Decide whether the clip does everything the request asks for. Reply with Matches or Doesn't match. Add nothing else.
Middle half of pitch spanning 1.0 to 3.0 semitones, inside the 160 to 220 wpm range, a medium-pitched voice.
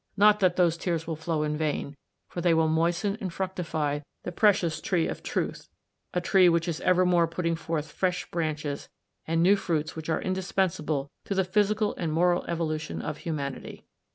Matches